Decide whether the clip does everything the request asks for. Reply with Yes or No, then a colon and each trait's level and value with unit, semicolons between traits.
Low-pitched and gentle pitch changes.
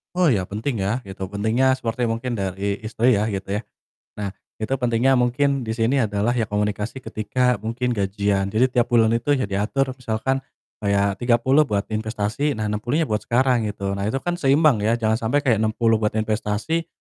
No: low, 115 Hz; average, 3.5 semitones